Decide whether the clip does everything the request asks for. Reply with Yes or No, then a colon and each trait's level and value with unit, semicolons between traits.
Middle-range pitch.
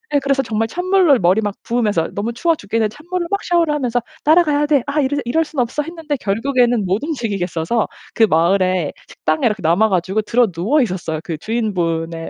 No: high, 230 Hz